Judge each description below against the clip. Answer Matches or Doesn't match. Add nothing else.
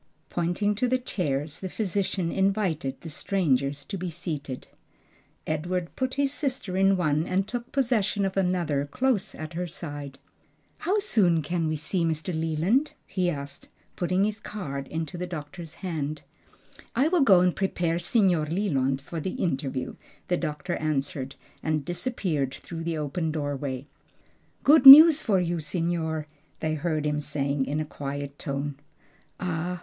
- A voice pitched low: Doesn't match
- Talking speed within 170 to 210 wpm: Doesn't match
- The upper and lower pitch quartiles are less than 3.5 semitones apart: Doesn't match